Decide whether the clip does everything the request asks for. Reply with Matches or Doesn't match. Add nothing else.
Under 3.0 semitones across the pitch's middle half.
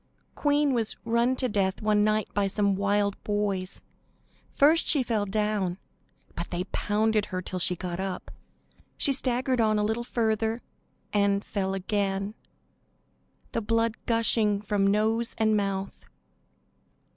Matches